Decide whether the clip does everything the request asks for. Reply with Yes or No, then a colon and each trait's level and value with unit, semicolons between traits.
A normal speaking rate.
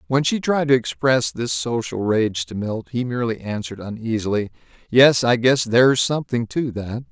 Yes: average, 175 wpm